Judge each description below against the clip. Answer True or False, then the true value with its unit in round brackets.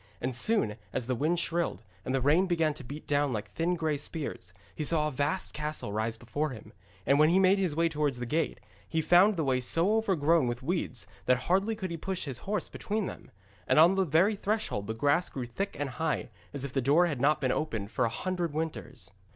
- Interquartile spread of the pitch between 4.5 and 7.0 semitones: True (5.2 semitones)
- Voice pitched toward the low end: False (150 Hz)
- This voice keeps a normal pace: False (230 wpm)